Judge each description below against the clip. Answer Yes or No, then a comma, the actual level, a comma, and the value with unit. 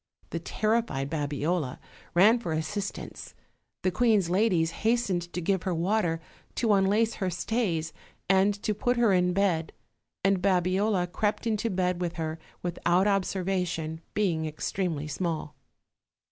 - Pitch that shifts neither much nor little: Yes, average, 3.7 semitones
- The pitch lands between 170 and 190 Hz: Yes, medium, 185 Hz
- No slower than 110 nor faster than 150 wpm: Yes, slow, 135 wpm